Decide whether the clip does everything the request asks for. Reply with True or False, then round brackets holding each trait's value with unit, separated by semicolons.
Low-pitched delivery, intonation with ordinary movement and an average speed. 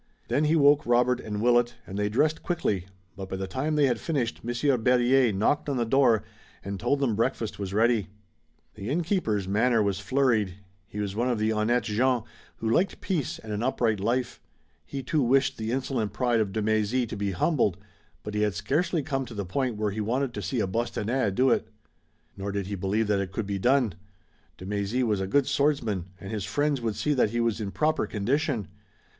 False (115 Hz; 4.3 semitones; 210 wpm)